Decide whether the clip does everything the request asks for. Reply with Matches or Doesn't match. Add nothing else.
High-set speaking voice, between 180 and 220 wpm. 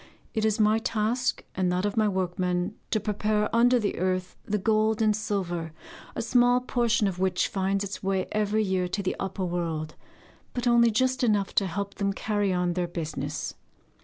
Matches